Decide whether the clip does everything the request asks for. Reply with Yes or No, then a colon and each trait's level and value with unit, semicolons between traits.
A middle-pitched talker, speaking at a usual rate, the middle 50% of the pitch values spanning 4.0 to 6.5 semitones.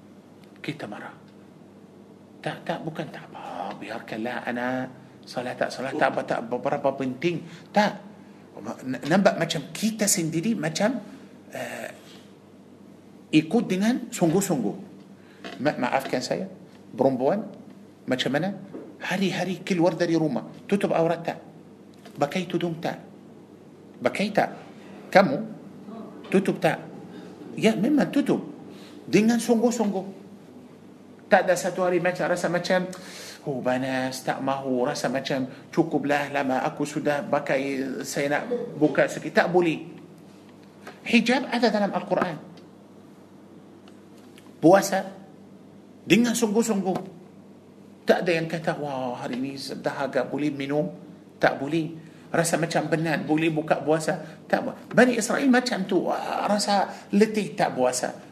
Yes: medium, 180 Hz; average, 120 wpm; wide, 5.5 semitones